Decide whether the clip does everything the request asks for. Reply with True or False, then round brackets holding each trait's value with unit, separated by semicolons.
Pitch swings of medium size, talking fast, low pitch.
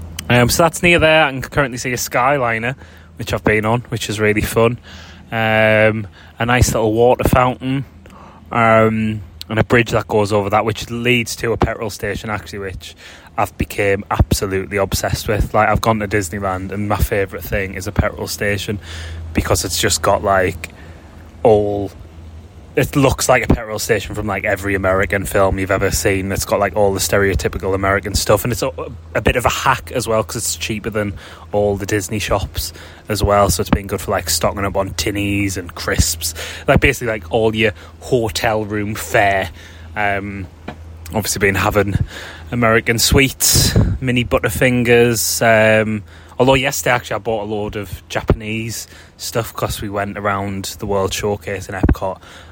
False (3.0 semitones; 175 wpm; 100 Hz)